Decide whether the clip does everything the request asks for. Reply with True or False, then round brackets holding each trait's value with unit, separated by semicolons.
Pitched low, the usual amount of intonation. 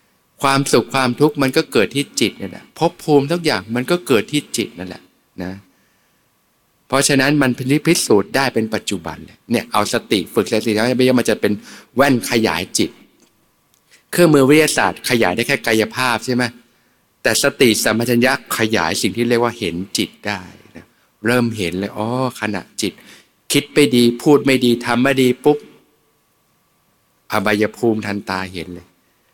True (120 Hz; 4.3 semitones)